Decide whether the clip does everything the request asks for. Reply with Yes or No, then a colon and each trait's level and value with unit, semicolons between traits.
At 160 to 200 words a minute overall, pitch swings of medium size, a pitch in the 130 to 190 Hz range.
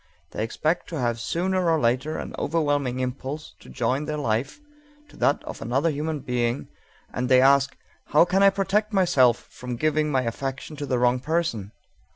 Yes: average, 180 wpm; average, 4.2 semitones; medium, 140 Hz